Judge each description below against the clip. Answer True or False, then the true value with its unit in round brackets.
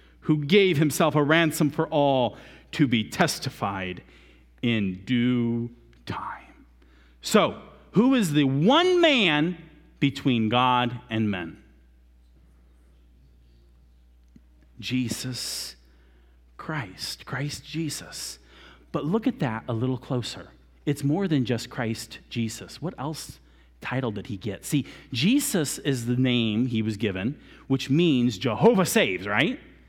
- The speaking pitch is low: True (120 Hz)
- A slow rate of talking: True (120 wpm)